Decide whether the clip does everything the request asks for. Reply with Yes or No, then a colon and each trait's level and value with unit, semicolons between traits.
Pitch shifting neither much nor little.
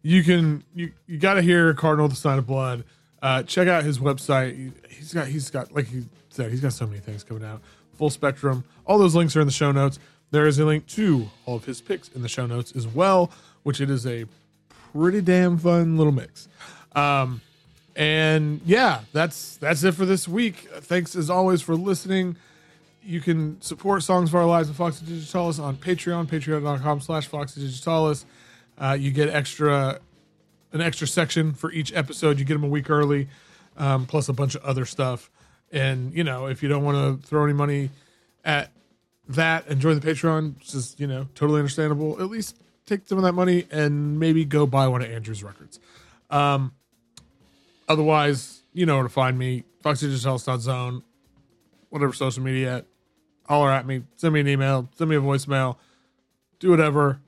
Yes: average, 3.4 semitones